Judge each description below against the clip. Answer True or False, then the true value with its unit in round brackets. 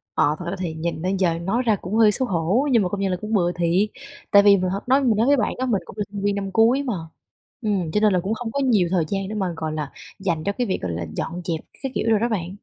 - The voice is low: False (195 Hz)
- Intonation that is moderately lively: True (4.1 semitones)